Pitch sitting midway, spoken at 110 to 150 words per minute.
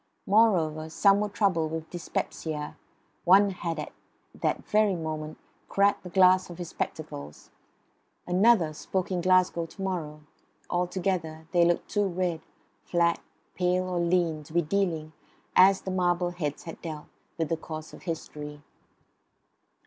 Yes: medium, 175 Hz; average, 140 wpm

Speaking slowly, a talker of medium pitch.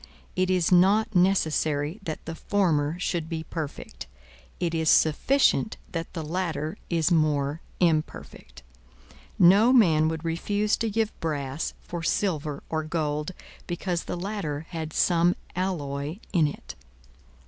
Yes: slow, 130 wpm; medium, 165 Hz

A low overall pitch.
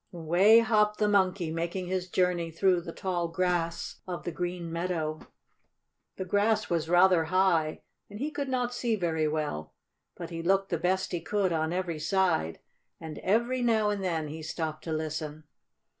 No: medium, 175 Hz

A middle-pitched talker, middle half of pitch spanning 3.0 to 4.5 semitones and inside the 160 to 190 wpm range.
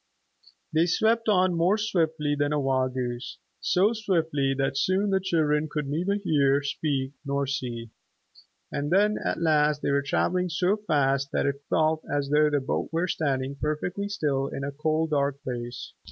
Yes: medium, 150 Hz; average, 4.1 semitones; average, 170 wpm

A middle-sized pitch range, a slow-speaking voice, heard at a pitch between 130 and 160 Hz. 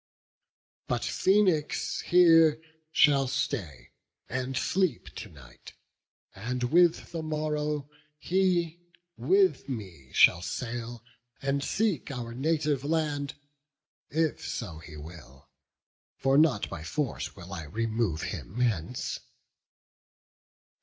No: wide, 6.8 semitones; slow, 105 wpm; low, 135 Hz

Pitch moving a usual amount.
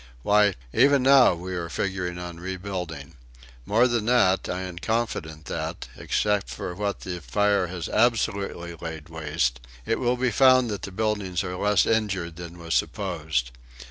Yes: average, 3.8 semitones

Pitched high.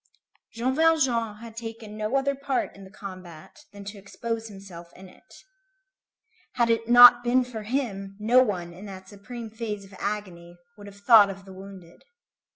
Yes: high, 210 Hz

